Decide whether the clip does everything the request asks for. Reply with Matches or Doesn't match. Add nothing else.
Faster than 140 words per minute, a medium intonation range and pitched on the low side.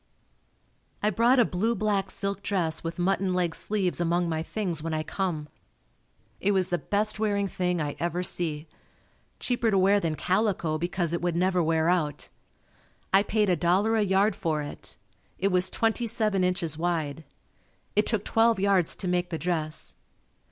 Doesn't match